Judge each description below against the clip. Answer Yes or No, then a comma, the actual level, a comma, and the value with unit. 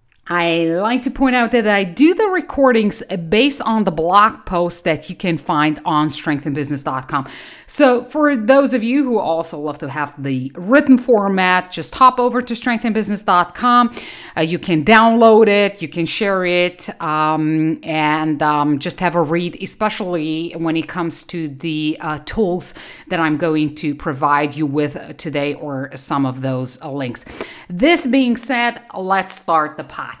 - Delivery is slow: No, average, 165 wpm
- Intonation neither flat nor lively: No, wide, 6.5 semitones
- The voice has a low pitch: No, medium, 175 Hz